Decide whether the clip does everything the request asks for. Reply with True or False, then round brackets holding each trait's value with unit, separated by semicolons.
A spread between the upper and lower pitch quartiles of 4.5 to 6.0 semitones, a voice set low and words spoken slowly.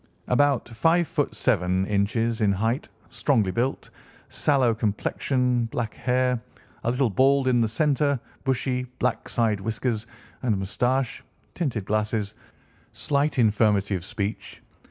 False (3.7 semitones; 115 Hz; 125 wpm)